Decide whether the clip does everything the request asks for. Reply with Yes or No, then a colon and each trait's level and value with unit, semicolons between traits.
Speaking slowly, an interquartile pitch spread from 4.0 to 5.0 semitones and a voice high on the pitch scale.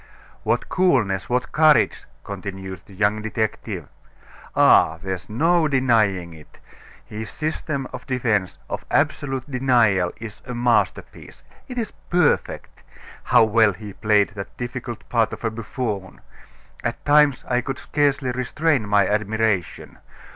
No: slow, 125 wpm; average, 4.6 semitones; low, 115 Hz